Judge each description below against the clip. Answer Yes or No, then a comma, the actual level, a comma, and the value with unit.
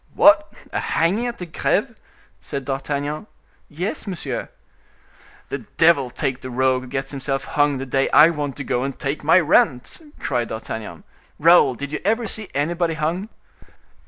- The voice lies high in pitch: No, medium, 145 Hz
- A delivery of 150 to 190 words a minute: Yes, average, 160 wpm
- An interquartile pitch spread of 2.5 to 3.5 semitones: No, average, 4.2 semitones